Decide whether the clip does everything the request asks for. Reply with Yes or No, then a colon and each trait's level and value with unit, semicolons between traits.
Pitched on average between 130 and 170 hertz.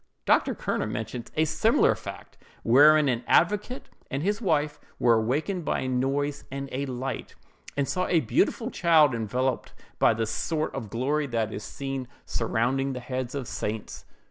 Yes: low, 135 Hz